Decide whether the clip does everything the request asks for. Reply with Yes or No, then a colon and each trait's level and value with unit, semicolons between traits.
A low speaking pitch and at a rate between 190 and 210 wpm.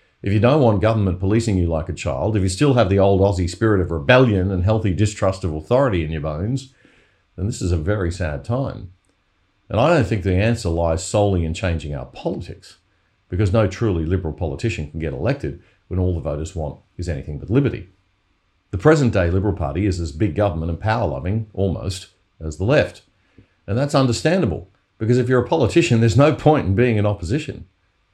Yes: very low, 95 Hz; fast, 205 wpm